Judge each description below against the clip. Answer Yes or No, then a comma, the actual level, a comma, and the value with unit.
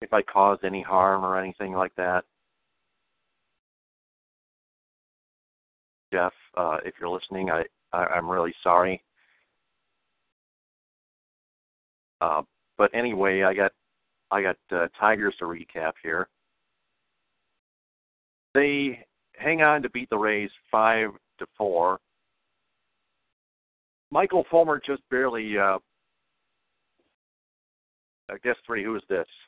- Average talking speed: No, slow, 105 wpm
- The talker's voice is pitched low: Yes, very low, 95 Hz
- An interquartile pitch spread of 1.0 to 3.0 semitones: No, average, 5.0 semitones